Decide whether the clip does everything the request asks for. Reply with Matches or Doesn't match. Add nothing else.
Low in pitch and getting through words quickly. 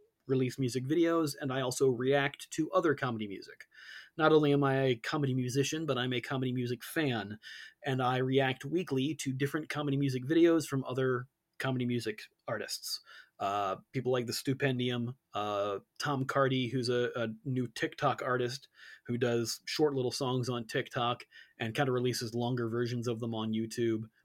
Doesn't match